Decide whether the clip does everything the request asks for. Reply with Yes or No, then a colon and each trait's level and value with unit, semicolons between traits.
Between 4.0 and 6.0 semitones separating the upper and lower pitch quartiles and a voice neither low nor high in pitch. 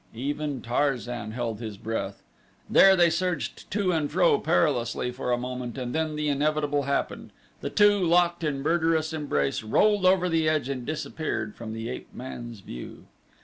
Yes: average, 5.3 semitones; medium, 145 Hz